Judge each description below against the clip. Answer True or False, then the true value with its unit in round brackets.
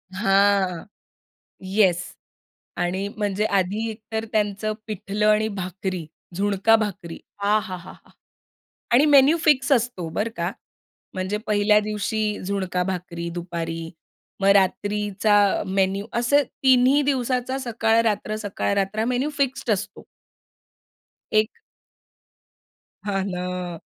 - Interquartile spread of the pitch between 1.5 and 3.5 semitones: True (3.0 semitones)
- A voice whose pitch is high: True (205 Hz)